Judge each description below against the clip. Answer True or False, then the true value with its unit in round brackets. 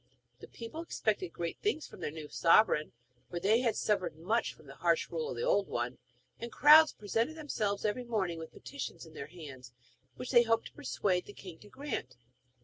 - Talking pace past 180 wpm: True (200 wpm)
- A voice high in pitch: True (215 Hz)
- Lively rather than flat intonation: True (7.2 semitones)